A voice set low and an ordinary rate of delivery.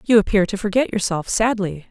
No: high, 205 Hz; average, 190 wpm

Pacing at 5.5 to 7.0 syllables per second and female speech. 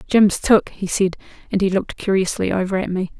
Yes: 5.6 syllables/s; female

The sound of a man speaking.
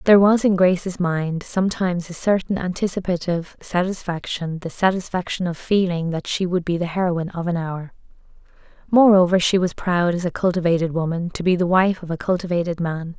No: female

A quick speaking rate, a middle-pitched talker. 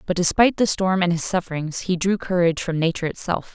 Yes: fast, 220 wpm; medium, 180 Hz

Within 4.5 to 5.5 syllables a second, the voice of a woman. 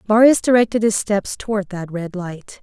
Yes: 4.9 syllables/s; female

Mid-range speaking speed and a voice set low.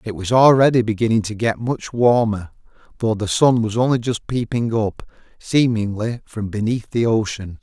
Yes: average, 165 wpm; low, 115 Hz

